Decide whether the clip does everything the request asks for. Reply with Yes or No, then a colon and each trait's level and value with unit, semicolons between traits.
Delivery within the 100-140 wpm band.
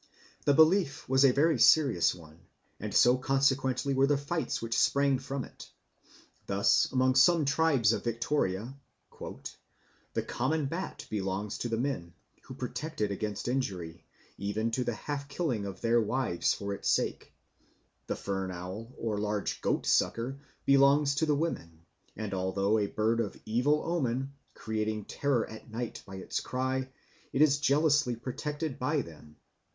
No: average, 155 wpm